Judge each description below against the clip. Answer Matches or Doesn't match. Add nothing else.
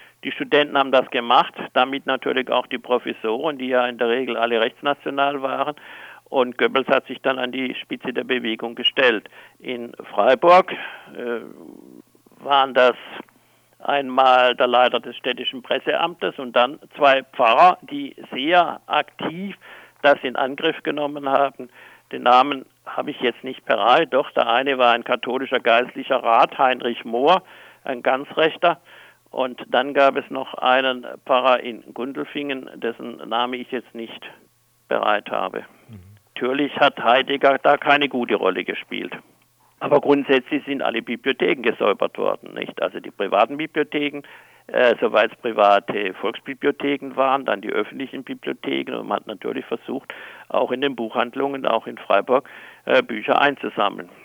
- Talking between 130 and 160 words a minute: Matches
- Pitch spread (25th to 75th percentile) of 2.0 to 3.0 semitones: Matches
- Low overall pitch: Matches